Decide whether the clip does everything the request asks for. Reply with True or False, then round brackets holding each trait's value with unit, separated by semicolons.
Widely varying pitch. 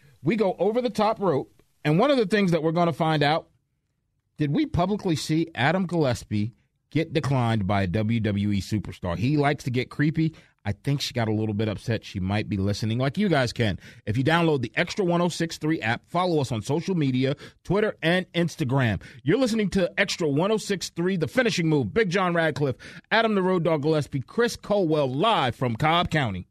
True (6.1 semitones)